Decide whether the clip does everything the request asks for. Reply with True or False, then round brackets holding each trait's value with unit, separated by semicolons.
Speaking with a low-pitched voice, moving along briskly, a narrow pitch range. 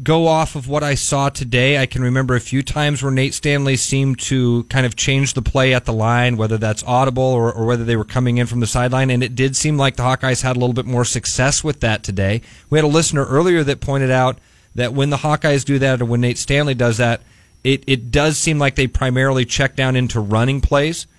True (130 Hz; 245 wpm; 2.3 semitones)